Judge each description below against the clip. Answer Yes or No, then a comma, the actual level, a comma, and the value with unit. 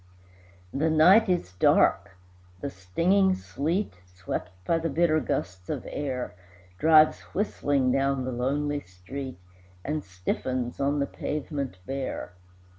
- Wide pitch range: No, average, 4.2 semitones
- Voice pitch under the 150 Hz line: Yes, medium, 140 Hz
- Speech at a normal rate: No, slow, 120 wpm